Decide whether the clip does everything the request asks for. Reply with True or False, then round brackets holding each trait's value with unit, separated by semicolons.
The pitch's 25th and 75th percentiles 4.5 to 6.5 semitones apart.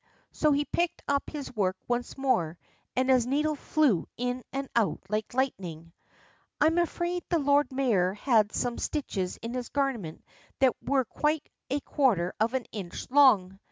True (5.3 semitones)